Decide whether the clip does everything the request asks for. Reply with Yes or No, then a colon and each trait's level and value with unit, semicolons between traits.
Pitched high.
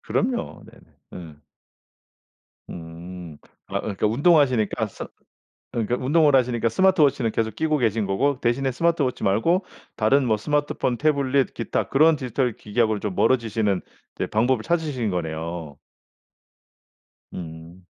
No: low, 120 Hz